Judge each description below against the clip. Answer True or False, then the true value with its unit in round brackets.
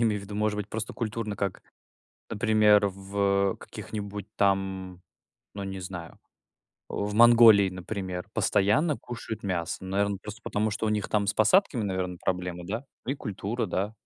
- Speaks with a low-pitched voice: True (100 Hz)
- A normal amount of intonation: False (2.1 semitones)